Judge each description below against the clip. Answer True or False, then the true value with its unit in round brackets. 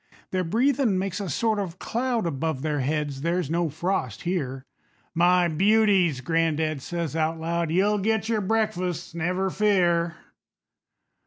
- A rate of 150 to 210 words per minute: False (140 wpm)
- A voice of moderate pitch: True (175 Hz)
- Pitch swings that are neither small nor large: True (3.8 semitones)